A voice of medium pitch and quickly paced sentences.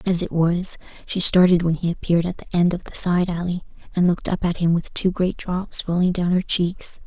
Yes: medium, 175 Hz; fast, 240 wpm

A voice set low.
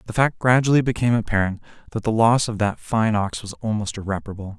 Yes: low, 110 Hz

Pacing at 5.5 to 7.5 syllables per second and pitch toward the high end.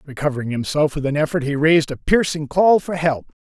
No: 5.9 syllables/s; medium, 150 Hz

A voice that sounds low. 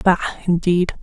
No: medium, 175 Hz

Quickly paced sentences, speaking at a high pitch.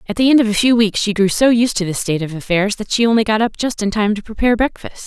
Yes: fast, 320 wpm; high, 215 Hz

